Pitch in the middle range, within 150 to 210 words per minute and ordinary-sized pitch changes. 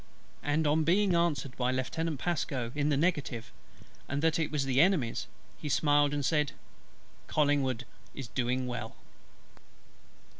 No: medium, 145 Hz; average, 140 wpm; average, 3.5 semitones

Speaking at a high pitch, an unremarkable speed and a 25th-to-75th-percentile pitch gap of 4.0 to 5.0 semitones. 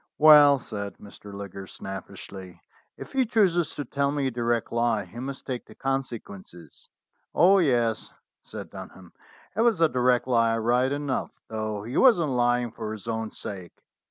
No: low, 120 Hz; average, 160 wpm; average, 4.7 semitones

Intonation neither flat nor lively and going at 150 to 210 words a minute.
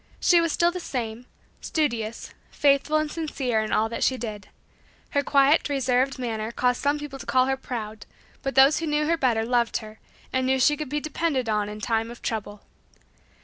Yes: average, 4.6 semitones; average, 195 wpm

